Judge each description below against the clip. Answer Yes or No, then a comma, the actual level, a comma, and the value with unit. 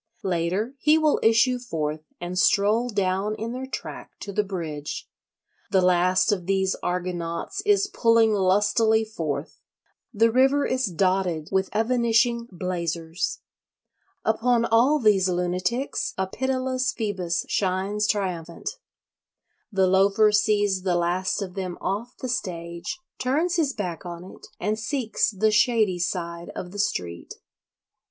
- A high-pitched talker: Yes, high, 200 Hz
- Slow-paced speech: Yes, slow, 130 wpm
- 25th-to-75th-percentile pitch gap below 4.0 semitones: No, average, 4.3 semitones